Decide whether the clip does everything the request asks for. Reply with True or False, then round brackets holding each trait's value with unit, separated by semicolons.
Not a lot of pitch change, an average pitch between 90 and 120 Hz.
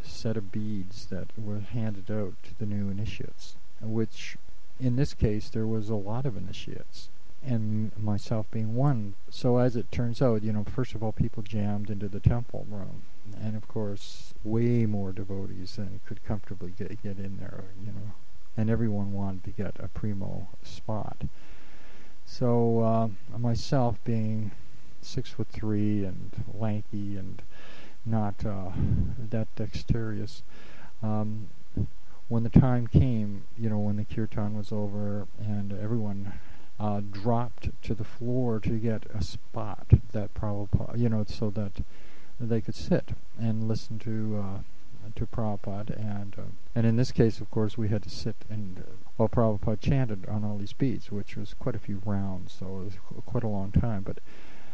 True (2.1 semitones; 105 Hz)